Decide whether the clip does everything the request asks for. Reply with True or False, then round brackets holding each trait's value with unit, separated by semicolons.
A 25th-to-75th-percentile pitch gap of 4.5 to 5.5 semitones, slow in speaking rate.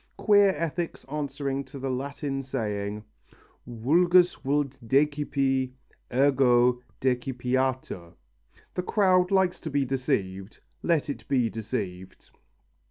False (3.3 semitones; 100 wpm)